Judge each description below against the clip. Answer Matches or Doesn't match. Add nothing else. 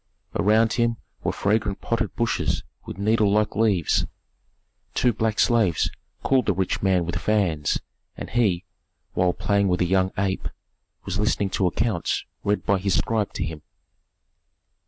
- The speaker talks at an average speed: Matches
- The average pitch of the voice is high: Doesn't match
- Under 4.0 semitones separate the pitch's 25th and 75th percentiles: Matches